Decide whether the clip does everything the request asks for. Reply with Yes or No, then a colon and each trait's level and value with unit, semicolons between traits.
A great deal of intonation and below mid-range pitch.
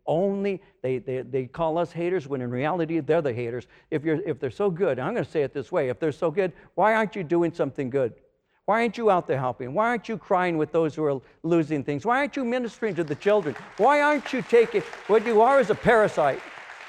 No: wide, 6.3 semitones; medium, 175 Hz